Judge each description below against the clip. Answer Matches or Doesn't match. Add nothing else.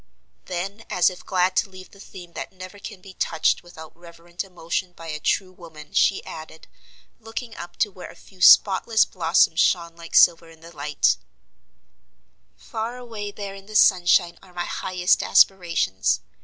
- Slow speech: Doesn't match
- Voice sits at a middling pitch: Matches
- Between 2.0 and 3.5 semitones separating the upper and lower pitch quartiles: Matches